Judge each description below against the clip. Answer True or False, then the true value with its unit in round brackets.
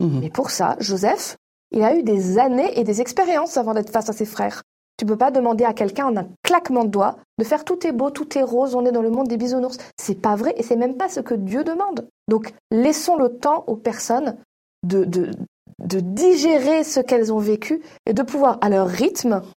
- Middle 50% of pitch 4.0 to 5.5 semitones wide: True (4.4 semitones)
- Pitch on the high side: True (240 Hz)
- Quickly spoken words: True (230 wpm)